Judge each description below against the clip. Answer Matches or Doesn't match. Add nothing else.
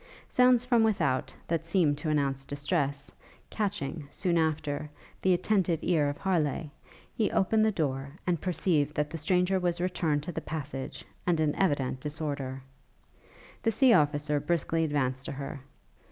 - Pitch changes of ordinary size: Matches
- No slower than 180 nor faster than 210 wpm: Doesn't match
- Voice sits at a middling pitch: Matches